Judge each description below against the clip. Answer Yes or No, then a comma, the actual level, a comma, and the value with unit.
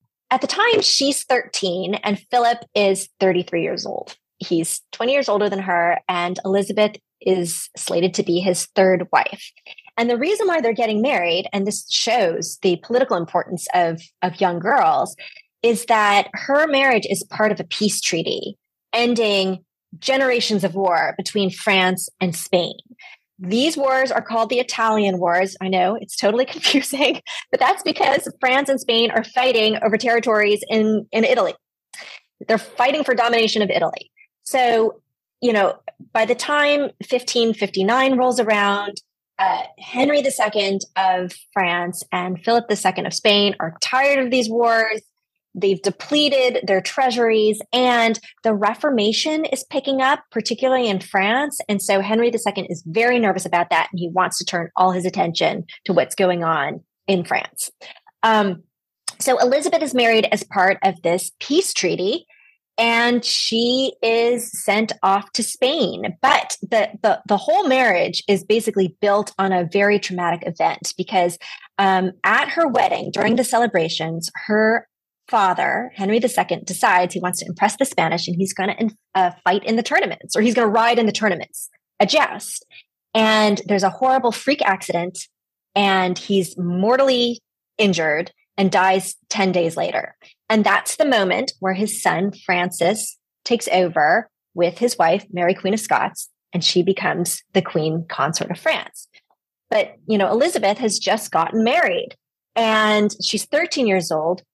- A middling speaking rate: Yes, average, 160 wpm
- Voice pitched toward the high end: Yes, high, 210 Hz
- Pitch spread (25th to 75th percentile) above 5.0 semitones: No, average, 4.6 semitones